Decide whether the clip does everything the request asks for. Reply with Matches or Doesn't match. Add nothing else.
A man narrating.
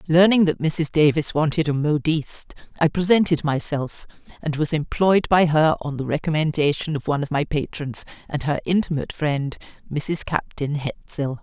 Doesn't match